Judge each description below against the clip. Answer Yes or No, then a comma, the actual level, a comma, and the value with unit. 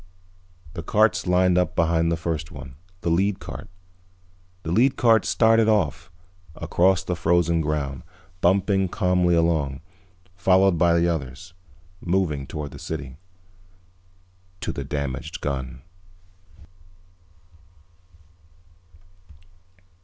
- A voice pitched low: Yes, very low, 85 Hz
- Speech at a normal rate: No, slow, 105 wpm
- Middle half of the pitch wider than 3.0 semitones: Yes, average, 3.5 semitones